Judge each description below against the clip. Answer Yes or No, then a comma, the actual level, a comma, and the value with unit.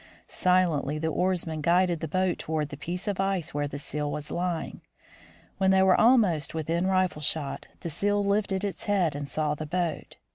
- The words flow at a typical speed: Yes, average, 185 wpm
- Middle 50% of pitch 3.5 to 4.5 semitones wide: Yes, average, 3.8 semitones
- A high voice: No, medium, 175 Hz